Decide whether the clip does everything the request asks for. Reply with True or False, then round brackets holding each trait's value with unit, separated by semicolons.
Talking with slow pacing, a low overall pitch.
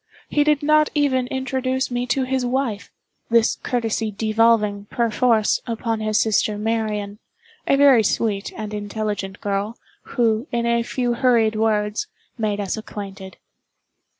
False (130 wpm; 225 Hz)